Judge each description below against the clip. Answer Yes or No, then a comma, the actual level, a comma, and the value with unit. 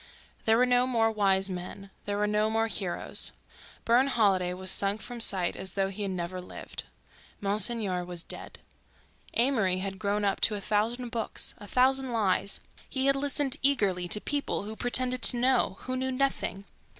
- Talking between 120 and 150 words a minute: No, average, 175 wpm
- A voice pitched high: Yes, high, 210 Hz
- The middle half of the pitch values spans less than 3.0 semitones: No, average, 4.4 semitones